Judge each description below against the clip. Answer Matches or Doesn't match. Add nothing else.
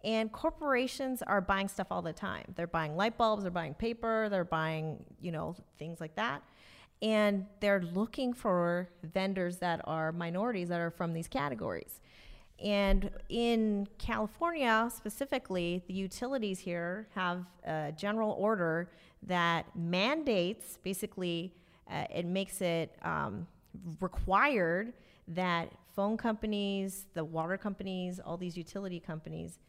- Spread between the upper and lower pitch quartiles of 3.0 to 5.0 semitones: Matches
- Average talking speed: Doesn't match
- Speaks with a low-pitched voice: Doesn't match